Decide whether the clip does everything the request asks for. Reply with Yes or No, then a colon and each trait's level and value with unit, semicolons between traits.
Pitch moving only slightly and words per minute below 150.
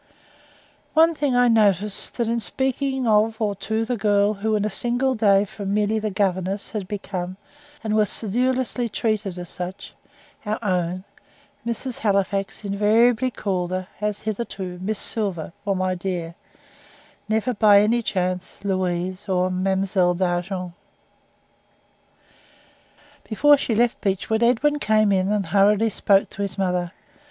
No: average, 3.0 semitones; average, 140 wpm